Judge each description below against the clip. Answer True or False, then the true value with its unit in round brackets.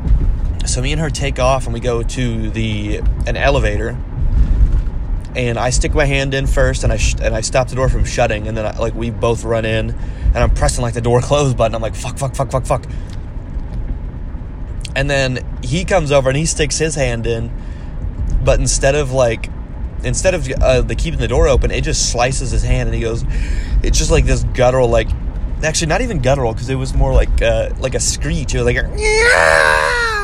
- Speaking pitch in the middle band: False (120 Hz)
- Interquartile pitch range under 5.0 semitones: True (3.5 semitones)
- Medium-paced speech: False (215 wpm)